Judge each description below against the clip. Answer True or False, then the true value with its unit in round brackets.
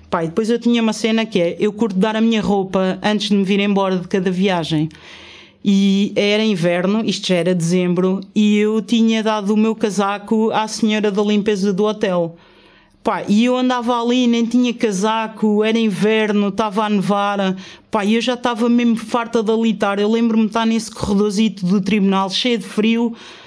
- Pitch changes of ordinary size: False (2.1 semitones)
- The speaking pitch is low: False (215 Hz)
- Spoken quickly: True (190 wpm)